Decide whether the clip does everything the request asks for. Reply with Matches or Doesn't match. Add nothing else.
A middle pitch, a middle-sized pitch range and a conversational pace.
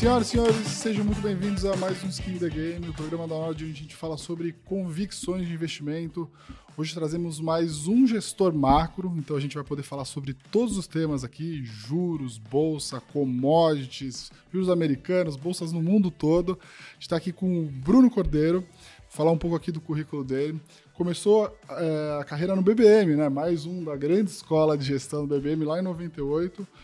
Matches